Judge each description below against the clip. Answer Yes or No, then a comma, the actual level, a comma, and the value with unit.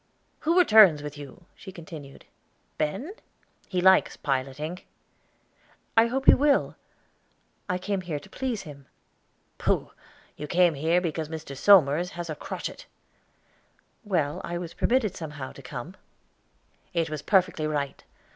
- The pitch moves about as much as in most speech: Yes, average, 4.3 semitones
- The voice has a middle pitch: Yes, medium, 170 Hz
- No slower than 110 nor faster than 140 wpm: Yes, slow, 135 wpm